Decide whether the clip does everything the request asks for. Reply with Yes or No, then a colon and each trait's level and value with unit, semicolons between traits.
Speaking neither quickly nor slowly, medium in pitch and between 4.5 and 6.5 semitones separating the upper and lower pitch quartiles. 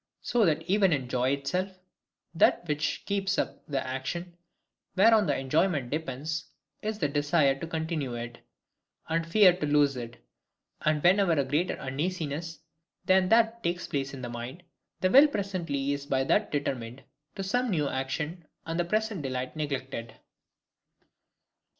Yes: average, 150 wpm; medium, 155 Hz; average, 5.2 semitones